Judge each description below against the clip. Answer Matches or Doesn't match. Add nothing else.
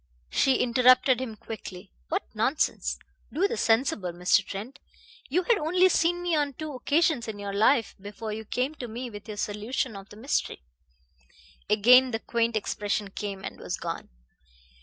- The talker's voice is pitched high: Matches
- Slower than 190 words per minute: Matches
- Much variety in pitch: Doesn't match